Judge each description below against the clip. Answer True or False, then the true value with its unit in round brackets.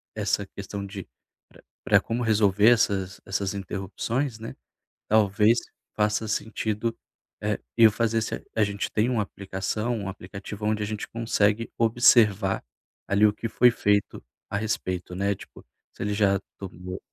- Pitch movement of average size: False (2.2 semitones)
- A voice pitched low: True (105 Hz)